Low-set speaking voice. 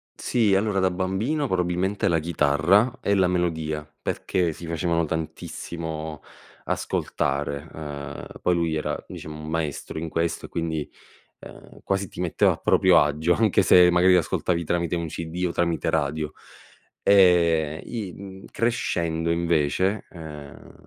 Yes: very low, 85 Hz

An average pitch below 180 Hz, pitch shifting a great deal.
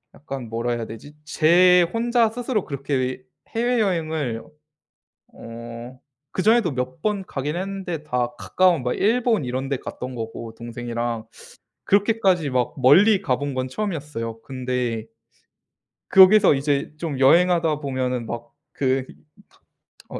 Yes: medium, 140 Hz; wide, 6.8 semitones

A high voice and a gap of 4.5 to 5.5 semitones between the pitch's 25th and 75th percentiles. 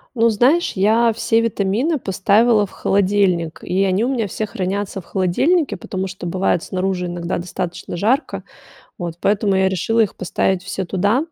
No: high, 195 Hz; average, 3.5 semitones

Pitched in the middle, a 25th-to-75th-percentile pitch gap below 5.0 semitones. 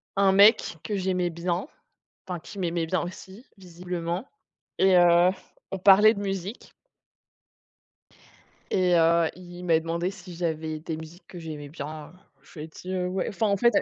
Yes: medium, 180 Hz; narrow, 2.4 semitones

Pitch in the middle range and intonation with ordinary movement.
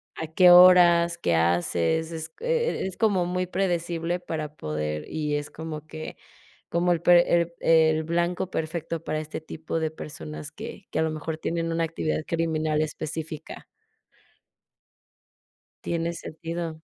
No: medium, 160 Hz; narrow, 1.7 semitones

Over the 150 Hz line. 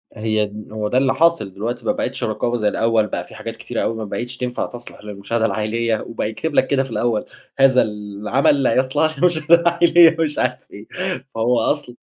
No: low, 120 Hz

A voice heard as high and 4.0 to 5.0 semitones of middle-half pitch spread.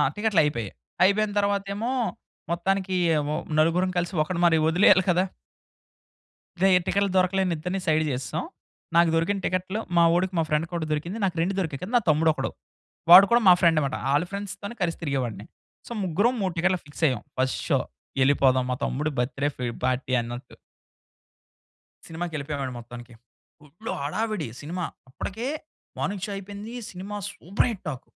No: medium, 175 Hz; average, 4.7 semitones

